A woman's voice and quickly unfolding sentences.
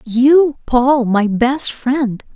No: female; slow, 125 wpm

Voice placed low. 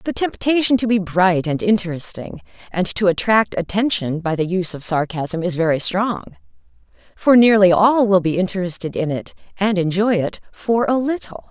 No: high, 190 Hz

